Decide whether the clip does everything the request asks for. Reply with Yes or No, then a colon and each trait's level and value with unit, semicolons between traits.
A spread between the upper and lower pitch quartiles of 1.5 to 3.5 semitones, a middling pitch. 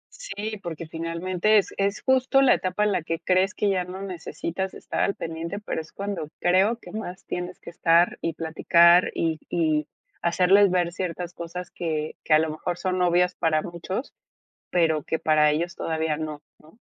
Yes: average, 2.7 semitones; medium, 175 Hz